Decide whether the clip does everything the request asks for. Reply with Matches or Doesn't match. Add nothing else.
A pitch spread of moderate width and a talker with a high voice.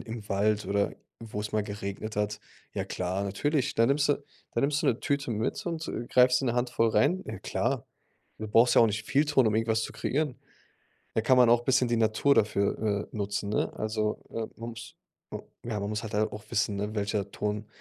Doesn't match